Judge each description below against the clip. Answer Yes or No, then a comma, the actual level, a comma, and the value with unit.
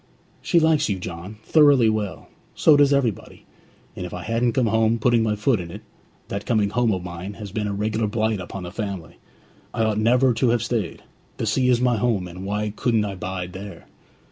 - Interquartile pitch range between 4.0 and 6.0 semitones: No, average, 3.3 semitones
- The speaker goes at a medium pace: No, fast, 210 wpm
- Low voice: Yes, low, 110 Hz